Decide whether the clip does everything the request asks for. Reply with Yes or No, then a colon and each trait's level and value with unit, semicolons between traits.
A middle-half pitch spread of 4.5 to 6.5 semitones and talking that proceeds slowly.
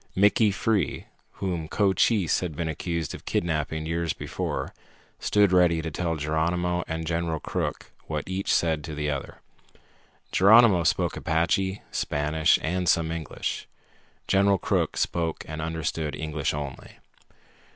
No: average, 2.8 semitones; slow, 130 wpm